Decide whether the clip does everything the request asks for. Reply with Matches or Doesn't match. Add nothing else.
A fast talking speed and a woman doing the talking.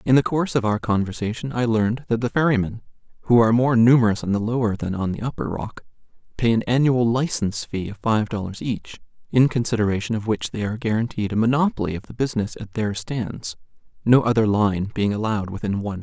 Doesn't match